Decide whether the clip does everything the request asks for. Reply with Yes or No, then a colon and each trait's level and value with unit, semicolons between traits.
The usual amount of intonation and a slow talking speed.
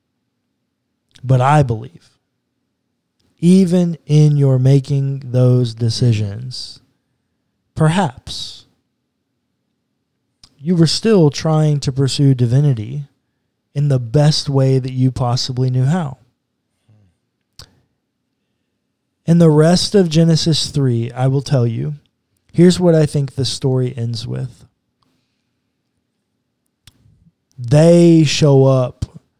Yes: average, 3.3 semitones; slow, 95 wpm